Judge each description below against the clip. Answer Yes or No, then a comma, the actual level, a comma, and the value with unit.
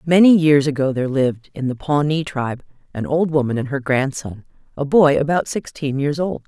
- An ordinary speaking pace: Yes, average, 195 wpm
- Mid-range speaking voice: Yes, medium, 145 Hz